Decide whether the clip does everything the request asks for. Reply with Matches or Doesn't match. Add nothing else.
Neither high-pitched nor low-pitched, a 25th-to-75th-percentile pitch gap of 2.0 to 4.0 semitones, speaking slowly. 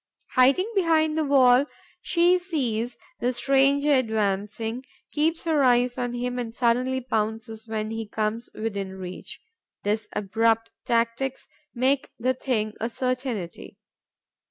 Doesn't match